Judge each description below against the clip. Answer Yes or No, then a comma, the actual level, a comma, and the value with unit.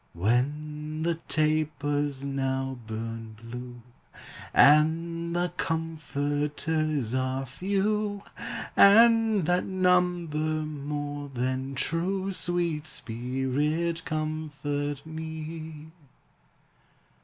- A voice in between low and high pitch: Yes, medium, 155 Hz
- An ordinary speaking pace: No, slow, 75 wpm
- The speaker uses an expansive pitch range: No, average, 3.5 semitones